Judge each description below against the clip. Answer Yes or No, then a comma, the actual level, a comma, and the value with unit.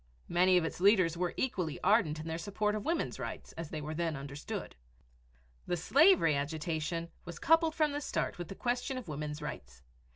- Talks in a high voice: No, medium, 170 Hz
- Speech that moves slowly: No, average, 190 wpm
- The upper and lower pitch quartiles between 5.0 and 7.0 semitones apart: Yes, wide, 5.6 semitones